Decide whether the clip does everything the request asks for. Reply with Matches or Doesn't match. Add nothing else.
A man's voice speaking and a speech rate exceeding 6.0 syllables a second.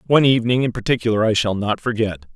Matches